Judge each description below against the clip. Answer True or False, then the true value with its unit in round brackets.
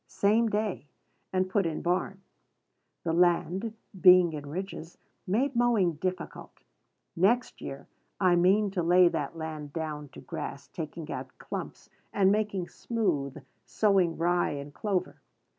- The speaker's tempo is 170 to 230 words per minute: False (135 wpm)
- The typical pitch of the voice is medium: True (180 Hz)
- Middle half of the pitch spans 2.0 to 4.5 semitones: True (3.6 semitones)